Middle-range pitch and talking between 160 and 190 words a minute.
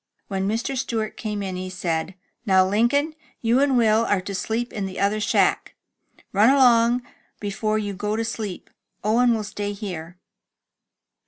No: high, 215 Hz; average, 165 wpm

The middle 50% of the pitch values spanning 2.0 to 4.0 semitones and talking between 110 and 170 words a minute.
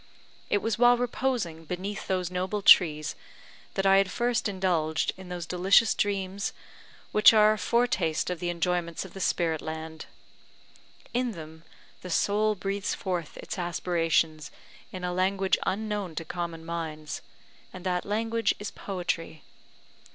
Yes: average, 3.5 semitones; average, 145 wpm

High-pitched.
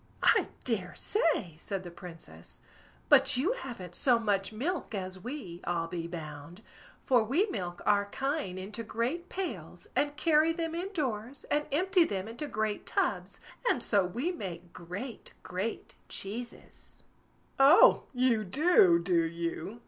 Yes: high, 220 Hz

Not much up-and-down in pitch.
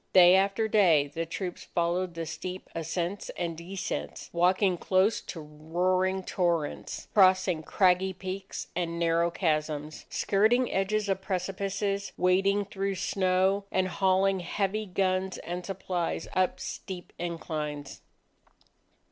Yes: narrow, 2.3 semitones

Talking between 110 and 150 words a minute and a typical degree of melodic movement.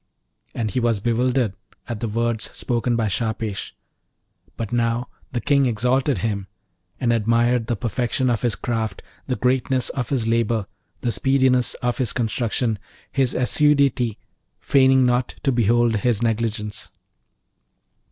No: slow, 135 wpm; narrow, 2.0 semitones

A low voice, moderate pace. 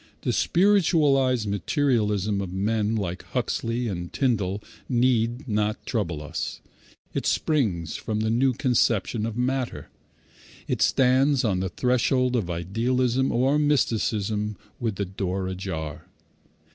No: low, 115 Hz; slow, 120 wpm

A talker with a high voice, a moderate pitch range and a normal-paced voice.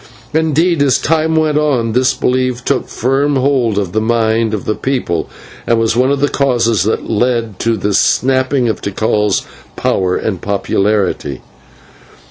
No: low, 120 Hz; average, 4.1 semitones; average, 155 wpm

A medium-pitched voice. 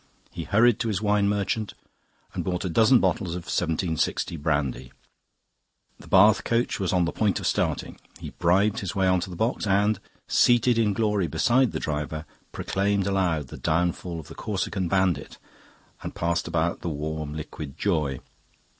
No: very low, 95 Hz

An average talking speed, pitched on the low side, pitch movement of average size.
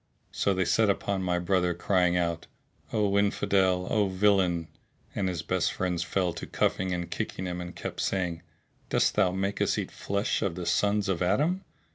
No: average, 180 wpm; very low, 95 Hz; narrow, 2.1 semitones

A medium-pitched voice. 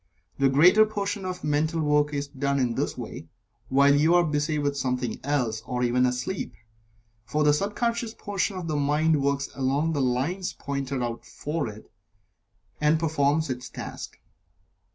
Yes: medium, 145 Hz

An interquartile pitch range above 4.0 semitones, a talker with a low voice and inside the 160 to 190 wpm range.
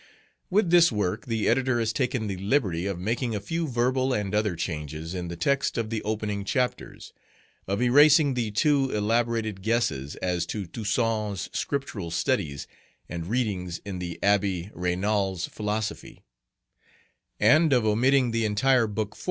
No: average, 4.8 semitones; low, 110 Hz; average, 150 wpm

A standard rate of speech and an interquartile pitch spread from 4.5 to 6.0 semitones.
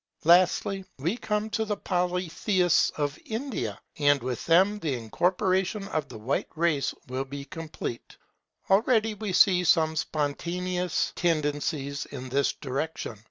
No: slow, 130 wpm; average, 5.2 semitones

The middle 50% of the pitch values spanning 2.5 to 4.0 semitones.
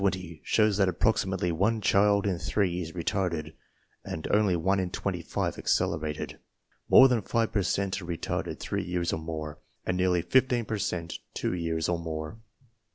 Yes: average, 3.4 semitones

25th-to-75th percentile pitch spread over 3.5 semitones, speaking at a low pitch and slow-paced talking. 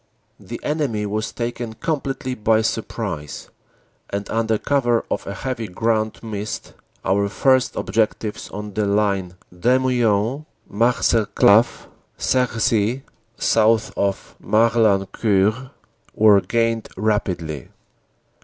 No: average, 2.7 semitones; low, 110 Hz; slow, 100 wpm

